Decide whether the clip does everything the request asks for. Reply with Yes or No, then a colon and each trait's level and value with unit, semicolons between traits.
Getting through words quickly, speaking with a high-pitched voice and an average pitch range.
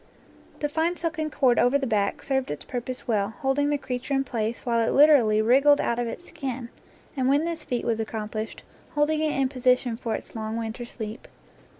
Yes: fast, 210 wpm; very high, 255 Hz; average, 4.0 semitones